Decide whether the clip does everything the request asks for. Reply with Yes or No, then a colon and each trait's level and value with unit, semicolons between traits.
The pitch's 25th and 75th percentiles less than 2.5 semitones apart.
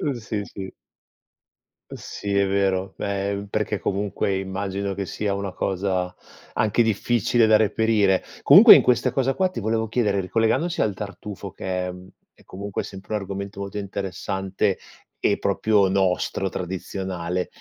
Yes: narrow, 2.1 semitones